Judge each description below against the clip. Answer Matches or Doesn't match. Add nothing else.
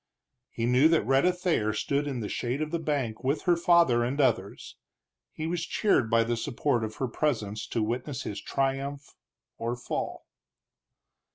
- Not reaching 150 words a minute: Doesn't match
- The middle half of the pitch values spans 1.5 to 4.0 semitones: Doesn't match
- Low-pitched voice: Matches